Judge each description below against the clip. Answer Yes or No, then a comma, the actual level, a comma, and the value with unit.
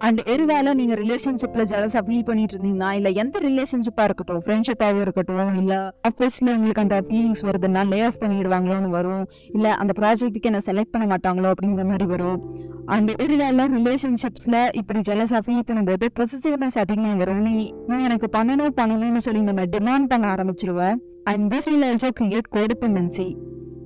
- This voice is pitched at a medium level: No, high, 215 Hz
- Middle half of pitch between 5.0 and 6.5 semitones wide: No, average, 3.7 semitones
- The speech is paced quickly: Yes, fast, 145 wpm